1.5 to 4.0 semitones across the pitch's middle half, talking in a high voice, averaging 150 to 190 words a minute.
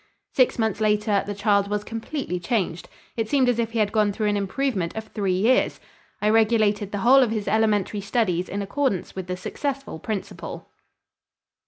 Yes: narrow, 2.4 semitones; high, 210 Hz; average, 180 wpm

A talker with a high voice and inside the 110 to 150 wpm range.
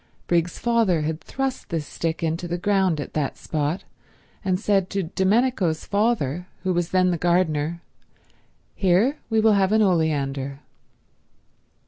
No: medium, 180 Hz; average, 140 wpm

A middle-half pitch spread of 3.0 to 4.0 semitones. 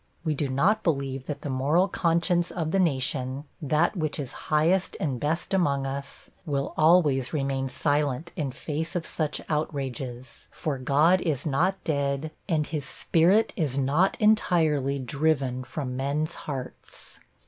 Yes: average, 3.3 semitones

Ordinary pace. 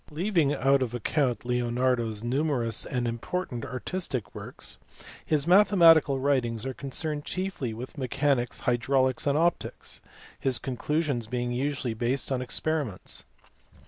No: slow, 125 wpm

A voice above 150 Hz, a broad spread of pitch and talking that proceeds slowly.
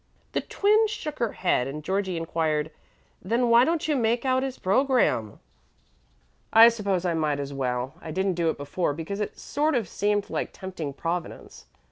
No: high, 190 Hz; wide, 7.2 semitones; average, 175 wpm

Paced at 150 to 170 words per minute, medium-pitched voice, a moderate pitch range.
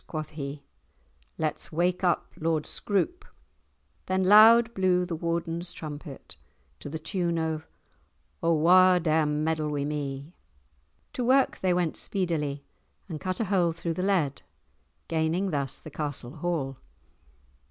No: slow, 135 wpm; medium, 165 Hz; average, 3.4 semitones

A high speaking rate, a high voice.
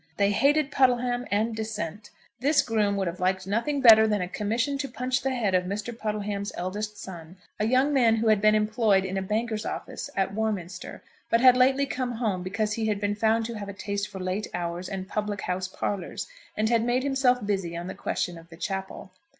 Yes: fast, 215 wpm; high, 210 Hz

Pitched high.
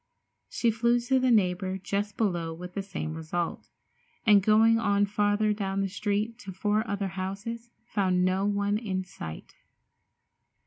Yes: high, 200 Hz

